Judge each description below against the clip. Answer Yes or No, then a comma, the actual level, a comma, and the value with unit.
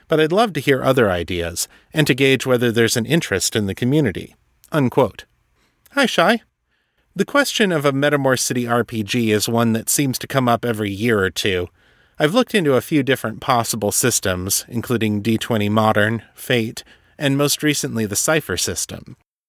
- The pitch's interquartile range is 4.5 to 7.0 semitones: Yes, average, 5.1 semitones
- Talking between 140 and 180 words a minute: Yes, average, 170 wpm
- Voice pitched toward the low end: Yes, low, 120 Hz